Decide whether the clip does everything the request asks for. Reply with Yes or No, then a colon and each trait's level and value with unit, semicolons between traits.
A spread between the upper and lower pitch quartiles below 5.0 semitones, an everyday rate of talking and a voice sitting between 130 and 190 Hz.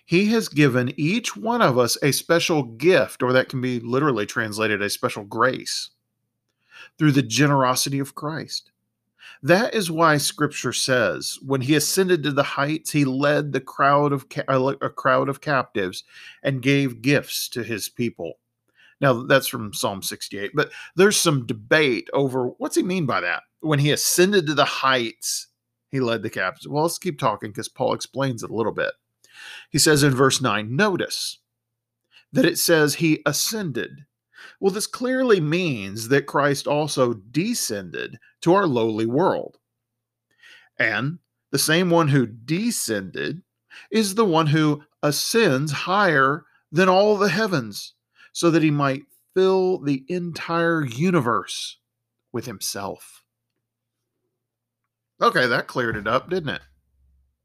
No: wide, 5.6 semitones; average, 150 wpm; medium, 140 Hz